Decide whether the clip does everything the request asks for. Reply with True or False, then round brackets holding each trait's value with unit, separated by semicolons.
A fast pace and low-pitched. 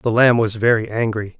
True (215 wpm; 110 Hz)